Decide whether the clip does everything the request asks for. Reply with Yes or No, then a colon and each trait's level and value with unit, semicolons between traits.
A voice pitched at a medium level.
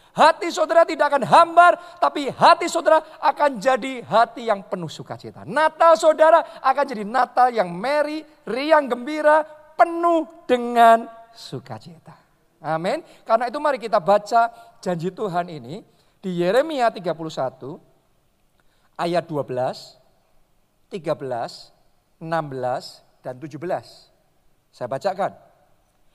No: high, 235 Hz